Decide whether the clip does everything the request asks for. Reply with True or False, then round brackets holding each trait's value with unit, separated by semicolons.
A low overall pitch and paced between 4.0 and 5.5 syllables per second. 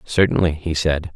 True (80 Hz; 4.8 syllables/s)